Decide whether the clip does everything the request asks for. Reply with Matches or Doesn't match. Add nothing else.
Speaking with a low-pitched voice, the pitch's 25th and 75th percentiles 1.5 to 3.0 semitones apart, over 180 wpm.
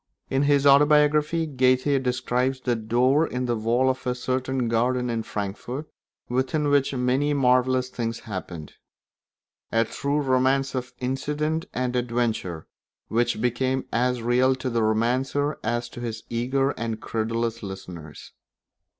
Doesn't match